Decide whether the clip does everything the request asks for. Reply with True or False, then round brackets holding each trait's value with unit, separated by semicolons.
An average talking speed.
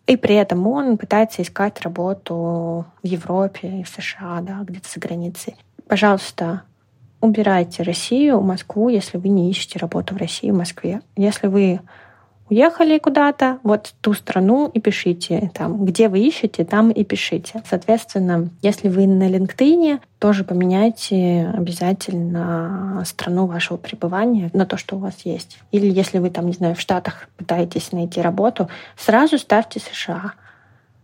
True (145 wpm)